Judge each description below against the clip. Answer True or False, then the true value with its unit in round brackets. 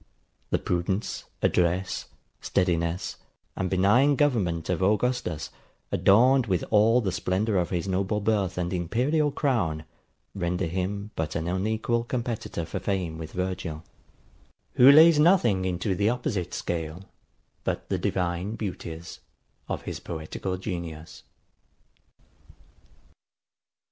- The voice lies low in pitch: True (95 Hz)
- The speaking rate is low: True (115 wpm)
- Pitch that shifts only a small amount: False (4.4 semitones)